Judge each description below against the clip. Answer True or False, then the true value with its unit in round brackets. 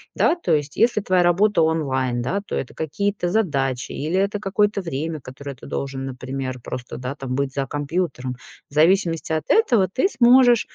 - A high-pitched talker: False (160 Hz)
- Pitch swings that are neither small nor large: False (6.7 semitones)